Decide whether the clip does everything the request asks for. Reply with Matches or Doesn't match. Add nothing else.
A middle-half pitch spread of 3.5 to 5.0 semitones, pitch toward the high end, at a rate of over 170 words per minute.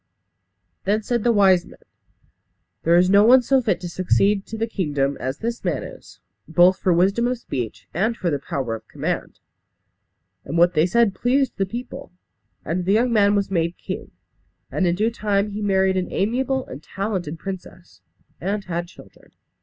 Matches